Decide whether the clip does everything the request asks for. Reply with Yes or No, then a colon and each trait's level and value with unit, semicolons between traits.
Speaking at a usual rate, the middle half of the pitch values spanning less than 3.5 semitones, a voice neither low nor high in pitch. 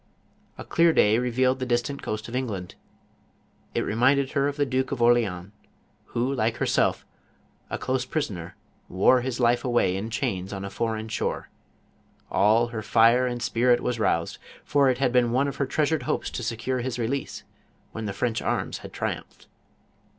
No: average, 180 wpm; average, 2.9 semitones; low, 120 Hz